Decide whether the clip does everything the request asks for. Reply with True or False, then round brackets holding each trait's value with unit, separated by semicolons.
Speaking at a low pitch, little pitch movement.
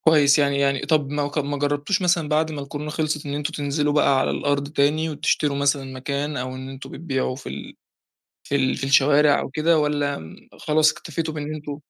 False (145 Hz; 1.5 semitones)